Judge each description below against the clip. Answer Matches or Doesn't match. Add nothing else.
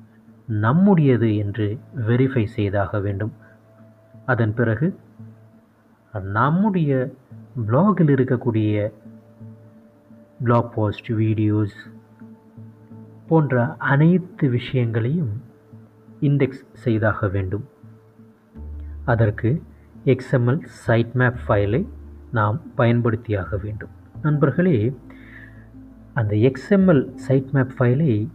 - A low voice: Matches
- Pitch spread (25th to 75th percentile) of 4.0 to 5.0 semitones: Doesn't match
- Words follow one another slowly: Matches